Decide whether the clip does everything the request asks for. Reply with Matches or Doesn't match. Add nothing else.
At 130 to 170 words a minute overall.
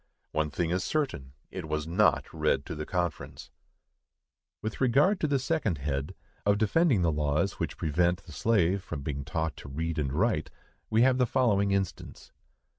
Matches